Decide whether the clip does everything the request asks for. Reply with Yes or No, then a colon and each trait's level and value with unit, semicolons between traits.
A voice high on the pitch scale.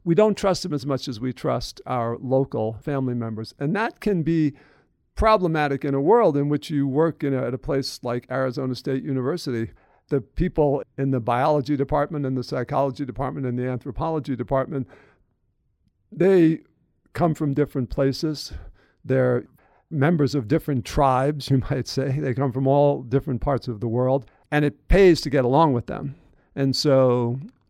No: low, 135 Hz